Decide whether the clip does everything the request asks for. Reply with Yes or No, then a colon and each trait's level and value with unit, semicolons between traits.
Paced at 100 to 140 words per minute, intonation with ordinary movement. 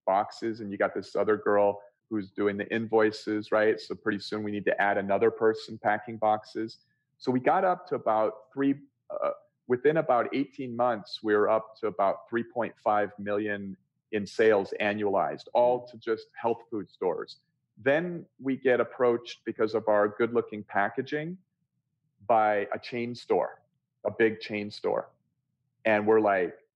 No: average, 160 wpm; average, 3.9 semitones